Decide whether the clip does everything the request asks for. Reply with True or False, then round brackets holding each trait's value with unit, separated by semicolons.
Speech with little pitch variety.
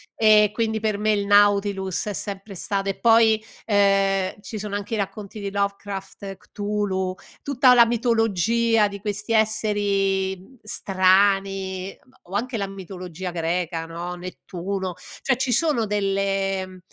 True (2.0 semitones)